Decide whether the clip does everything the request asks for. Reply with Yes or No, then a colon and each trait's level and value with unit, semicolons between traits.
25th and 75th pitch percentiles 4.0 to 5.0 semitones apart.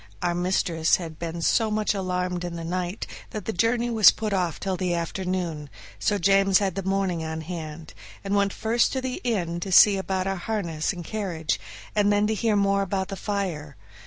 No: average, 3.0 semitones